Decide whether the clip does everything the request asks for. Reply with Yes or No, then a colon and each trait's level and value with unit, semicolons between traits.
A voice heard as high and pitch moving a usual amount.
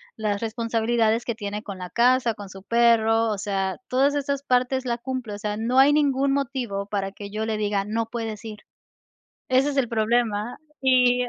Yes: high, 230 Hz; average, 3.2 semitones